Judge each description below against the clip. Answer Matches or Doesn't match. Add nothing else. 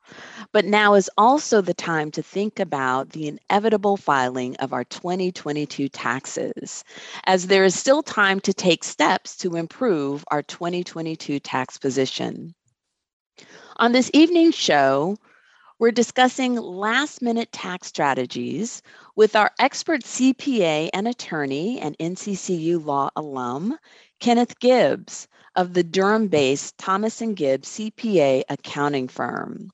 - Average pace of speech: Doesn't match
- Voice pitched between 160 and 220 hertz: Matches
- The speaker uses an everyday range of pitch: Doesn't match